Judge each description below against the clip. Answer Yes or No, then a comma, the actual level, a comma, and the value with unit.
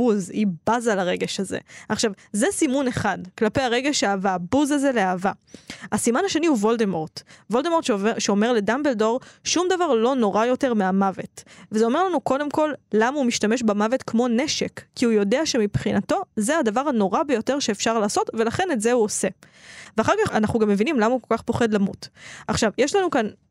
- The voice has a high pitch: Yes, high, 230 Hz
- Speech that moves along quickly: Yes, fast, 175 wpm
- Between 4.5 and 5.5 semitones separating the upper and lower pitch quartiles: No, average, 4.0 semitones